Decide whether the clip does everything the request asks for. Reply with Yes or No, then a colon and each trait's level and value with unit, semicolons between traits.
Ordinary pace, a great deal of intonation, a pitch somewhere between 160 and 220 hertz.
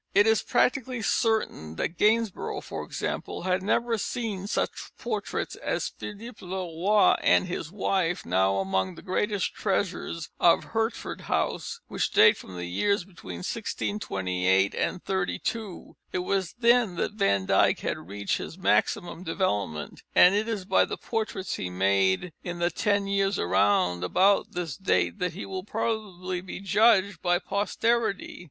No: average, 150 wpm; average, 4.6 semitones; medium, 185 Hz